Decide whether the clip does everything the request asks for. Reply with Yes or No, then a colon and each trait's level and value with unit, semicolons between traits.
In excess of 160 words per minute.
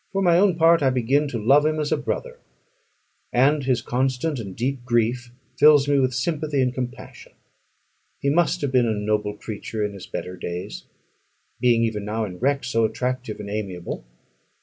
Yes: average, 180 wpm